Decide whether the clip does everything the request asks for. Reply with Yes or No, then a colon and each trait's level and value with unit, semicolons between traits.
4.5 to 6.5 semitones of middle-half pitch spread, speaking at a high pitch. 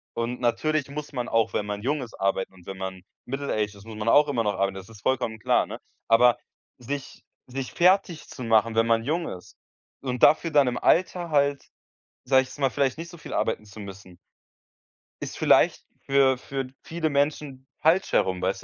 No: average, 4.9 semitones; low, 125 Hz